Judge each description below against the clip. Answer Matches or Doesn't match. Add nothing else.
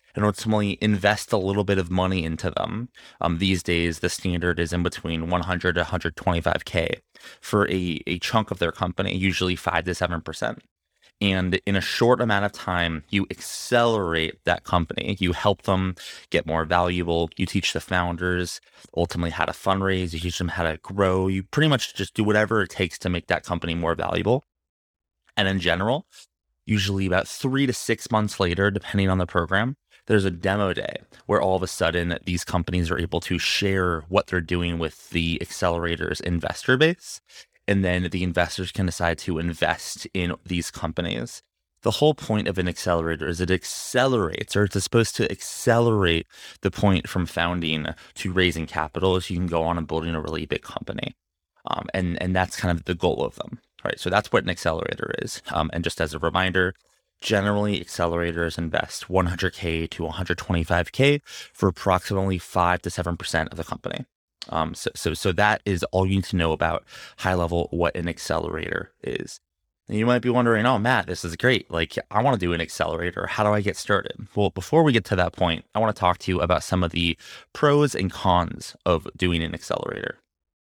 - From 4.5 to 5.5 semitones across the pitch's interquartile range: Doesn't match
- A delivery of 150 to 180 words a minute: Doesn't match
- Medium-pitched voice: Doesn't match